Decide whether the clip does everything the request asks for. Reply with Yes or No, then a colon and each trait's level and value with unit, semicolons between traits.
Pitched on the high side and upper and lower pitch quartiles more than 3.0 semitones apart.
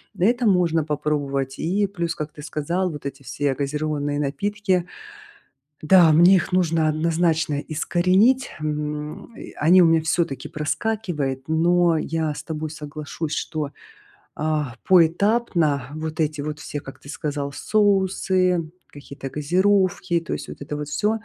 No: medium, 160 Hz; average, 3.4 semitones